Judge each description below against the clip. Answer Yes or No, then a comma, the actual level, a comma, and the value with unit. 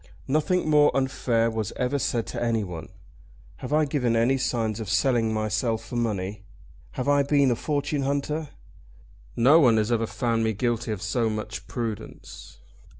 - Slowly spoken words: No, average, 160 wpm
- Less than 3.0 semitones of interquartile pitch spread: No, average, 3.9 semitones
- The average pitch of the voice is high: No, low, 120 Hz